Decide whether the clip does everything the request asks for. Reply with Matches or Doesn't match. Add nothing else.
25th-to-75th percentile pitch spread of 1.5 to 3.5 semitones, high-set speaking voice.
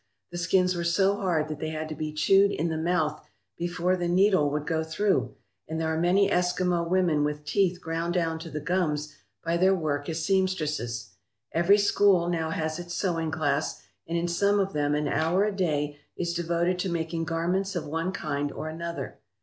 Doesn't match